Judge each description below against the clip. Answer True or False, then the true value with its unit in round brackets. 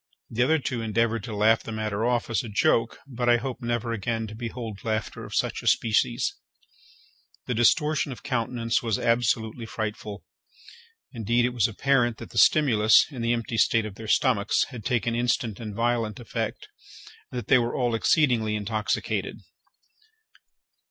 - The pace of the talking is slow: False (165 wpm)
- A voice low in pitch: True (115 Hz)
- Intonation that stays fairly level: True (1.9 semitones)